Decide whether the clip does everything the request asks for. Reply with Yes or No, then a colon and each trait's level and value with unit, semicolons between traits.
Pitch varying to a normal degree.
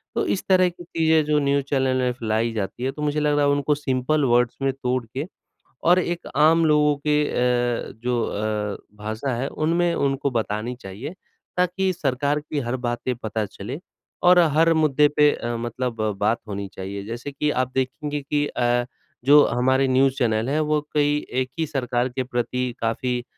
Yes: average, 3.7 semitones